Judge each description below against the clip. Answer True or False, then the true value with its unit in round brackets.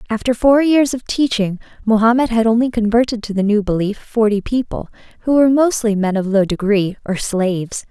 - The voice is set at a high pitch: True (225 Hz)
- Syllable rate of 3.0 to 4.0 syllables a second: False (5.4 syllables/s)